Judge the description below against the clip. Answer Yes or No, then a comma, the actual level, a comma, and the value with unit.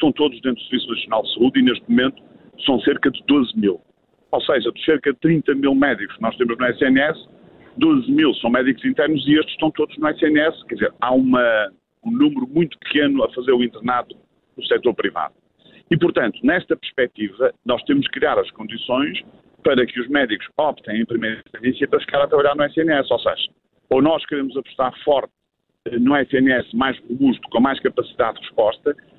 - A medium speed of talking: No, fast, 195 wpm